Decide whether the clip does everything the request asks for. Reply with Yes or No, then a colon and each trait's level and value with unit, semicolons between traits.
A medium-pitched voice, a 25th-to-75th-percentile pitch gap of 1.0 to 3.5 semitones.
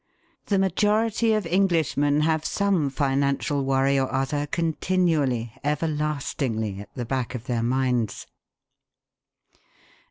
No: medium, 145 Hz; average, 4.1 semitones